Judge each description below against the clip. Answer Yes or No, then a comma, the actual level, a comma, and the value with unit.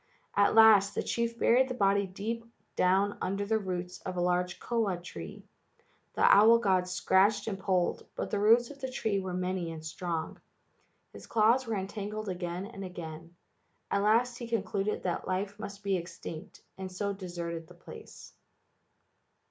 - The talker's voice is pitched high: Yes, high, 195 Hz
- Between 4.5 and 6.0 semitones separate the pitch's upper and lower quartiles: No, average, 3.1 semitones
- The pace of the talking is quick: No, average, 165 wpm